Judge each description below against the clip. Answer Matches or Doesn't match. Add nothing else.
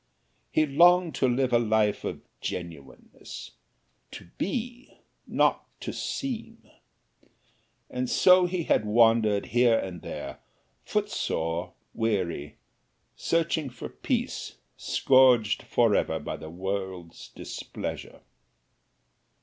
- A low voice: Matches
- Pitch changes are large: Matches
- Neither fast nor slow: Doesn't match